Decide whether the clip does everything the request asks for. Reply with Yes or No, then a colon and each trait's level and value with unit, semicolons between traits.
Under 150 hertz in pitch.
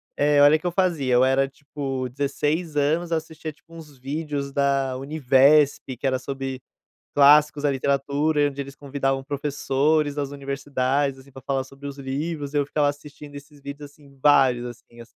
Yes: medium, 140 Hz